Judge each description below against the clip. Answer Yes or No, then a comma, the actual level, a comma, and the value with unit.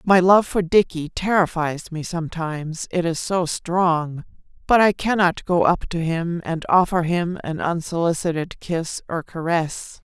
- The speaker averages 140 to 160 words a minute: Yes, average, 155 wpm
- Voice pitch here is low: No, medium, 170 Hz